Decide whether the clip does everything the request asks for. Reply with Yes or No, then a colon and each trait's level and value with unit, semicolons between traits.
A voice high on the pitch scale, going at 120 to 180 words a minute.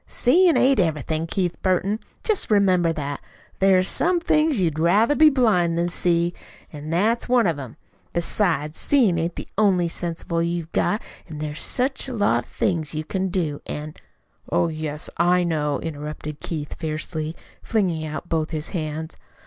No: medium, 170 Hz; average, 170 wpm